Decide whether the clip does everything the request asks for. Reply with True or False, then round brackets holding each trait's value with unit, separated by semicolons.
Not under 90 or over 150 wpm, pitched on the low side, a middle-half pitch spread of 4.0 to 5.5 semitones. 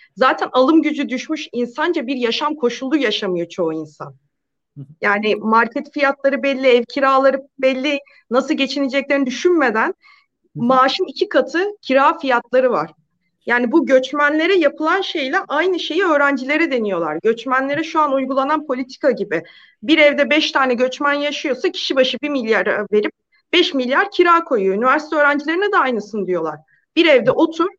False (140 wpm; 275 Hz; 4.4 semitones)